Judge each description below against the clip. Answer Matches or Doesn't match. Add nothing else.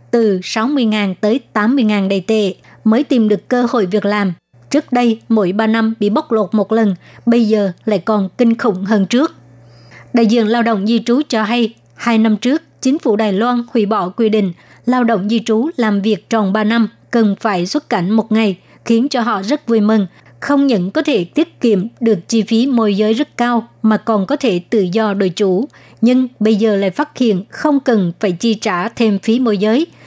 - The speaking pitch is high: Matches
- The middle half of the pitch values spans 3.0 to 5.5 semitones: Doesn't match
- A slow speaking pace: Doesn't match